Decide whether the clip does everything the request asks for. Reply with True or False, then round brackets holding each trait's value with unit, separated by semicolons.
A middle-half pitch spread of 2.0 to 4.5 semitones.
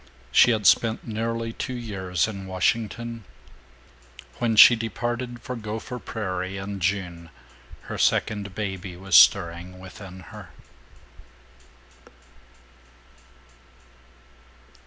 True (3.7 semitones)